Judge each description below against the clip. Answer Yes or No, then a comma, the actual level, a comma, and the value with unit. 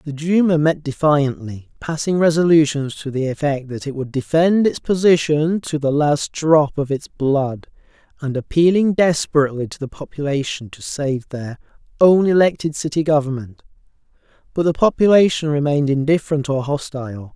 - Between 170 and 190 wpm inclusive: No, average, 145 wpm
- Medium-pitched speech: Yes, medium, 150 Hz